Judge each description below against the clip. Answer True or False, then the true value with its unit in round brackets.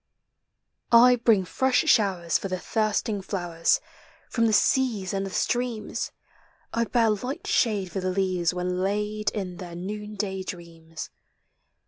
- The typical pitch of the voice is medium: False (195 Hz)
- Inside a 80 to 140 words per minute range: True (135 wpm)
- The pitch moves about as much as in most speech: True (3.3 semitones)